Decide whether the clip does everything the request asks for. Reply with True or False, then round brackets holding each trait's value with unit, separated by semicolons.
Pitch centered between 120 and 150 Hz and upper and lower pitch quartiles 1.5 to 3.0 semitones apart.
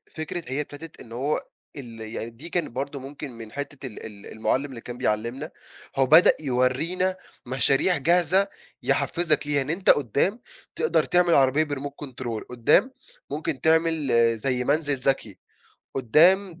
False (140 Hz; 4.4 semitones)